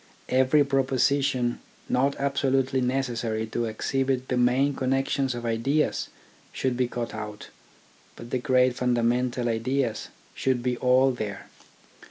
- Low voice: Yes, low, 125 Hz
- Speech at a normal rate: No, slow, 125 wpm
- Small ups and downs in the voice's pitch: Yes, narrow, 1.9 semitones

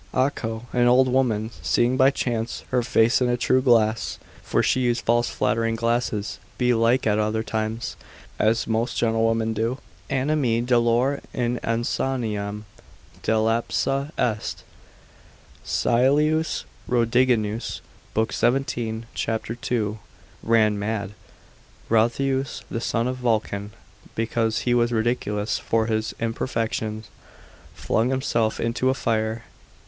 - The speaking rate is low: Yes, slow, 115 wpm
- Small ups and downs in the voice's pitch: Yes, narrow, 1.9 semitones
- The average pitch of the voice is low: Yes, low, 115 Hz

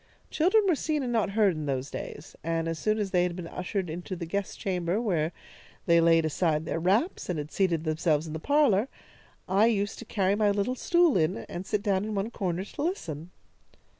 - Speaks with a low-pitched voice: No, high, 190 Hz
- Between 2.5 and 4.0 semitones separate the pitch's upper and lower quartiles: No, average, 4.6 semitones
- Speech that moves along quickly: Yes, fast, 215 wpm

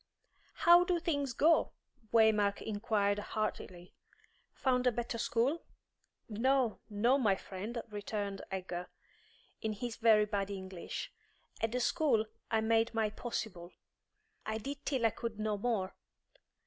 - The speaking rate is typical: No, slow, 130 wpm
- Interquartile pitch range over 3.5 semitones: No, average, 3.1 semitones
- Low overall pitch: No, high, 220 Hz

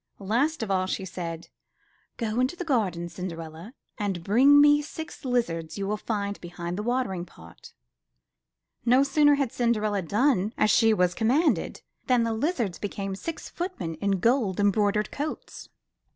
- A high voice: Yes, high, 210 Hz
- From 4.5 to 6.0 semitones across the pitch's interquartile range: Yes, wide, 5.6 semitones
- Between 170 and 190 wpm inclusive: No, average, 160 wpm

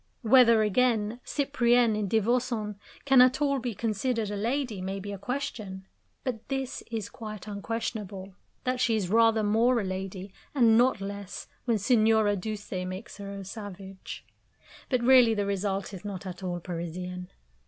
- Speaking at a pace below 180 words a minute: Yes, average, 160 wpm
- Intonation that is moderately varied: Yes, average, 3.5 semitones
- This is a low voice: No, high, 215 Hz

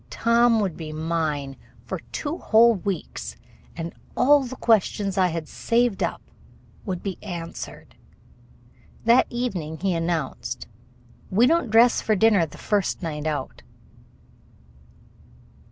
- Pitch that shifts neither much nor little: No, wide, 5.9 semitones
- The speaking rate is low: Yes, slow, 120 wpm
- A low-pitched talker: No, high, 195 Hz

